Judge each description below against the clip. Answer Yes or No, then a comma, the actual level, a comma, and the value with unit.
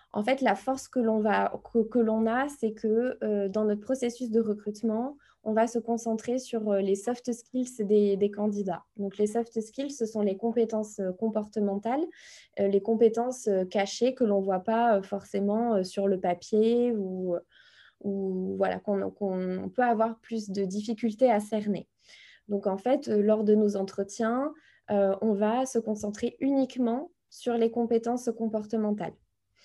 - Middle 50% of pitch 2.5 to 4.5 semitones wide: Yes, average, 2.8 semitones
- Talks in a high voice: Yes, high, 220 Hz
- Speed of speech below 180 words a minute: Yes, average, 165 wpm